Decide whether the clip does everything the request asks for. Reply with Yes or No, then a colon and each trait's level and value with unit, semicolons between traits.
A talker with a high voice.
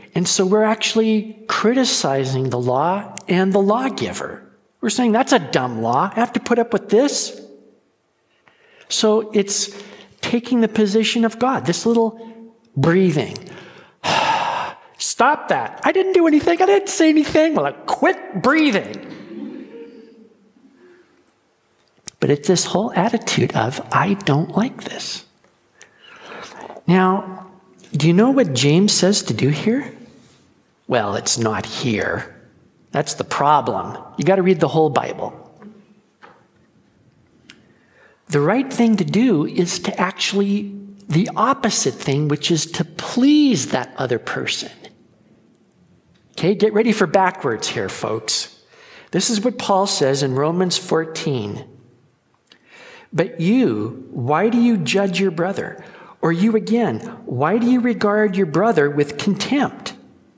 Yes: high, 205 Hz